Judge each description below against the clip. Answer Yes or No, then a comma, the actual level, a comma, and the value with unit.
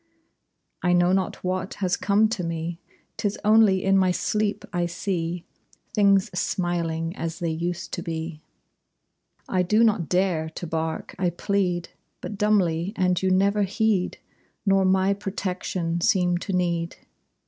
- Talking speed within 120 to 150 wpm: Yes, average, 145 wpm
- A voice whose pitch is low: No, medium, 180 Hz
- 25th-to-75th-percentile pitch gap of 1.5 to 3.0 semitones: Yes, narrow, 2.4 semitones